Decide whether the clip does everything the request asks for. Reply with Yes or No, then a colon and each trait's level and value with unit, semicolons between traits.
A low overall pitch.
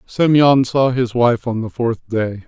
Yes: low, 120 Hz